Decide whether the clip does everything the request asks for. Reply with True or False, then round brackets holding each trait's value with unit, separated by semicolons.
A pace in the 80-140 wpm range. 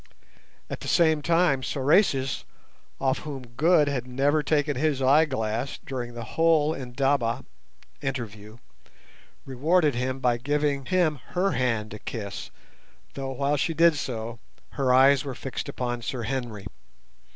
True (135 wpm)